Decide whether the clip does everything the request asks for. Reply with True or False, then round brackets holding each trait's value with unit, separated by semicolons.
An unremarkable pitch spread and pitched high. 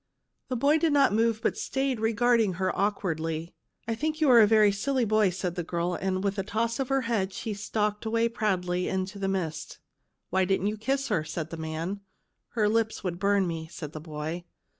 True (4.3 semitones; 200 Hz)